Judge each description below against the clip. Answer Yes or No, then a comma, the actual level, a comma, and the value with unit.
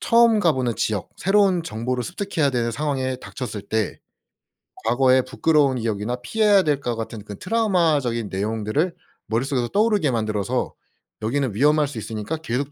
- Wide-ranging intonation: Yes, wide, 6.2 semitones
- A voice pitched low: Yes, low, 130 Hz